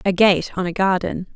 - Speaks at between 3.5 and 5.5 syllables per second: Yes, 5.0 syllables/s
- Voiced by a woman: Yes, female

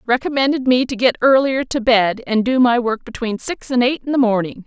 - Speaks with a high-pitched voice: Yes, high, 245 Hz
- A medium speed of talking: No, fast, 230 wpm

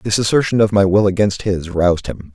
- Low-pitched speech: Yes, low, 100 Hz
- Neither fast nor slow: No, fast, 230 wpm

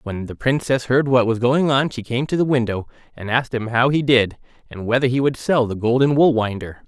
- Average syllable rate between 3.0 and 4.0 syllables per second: No, 5.5 syllables/s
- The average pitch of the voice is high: No, low, 125 Hz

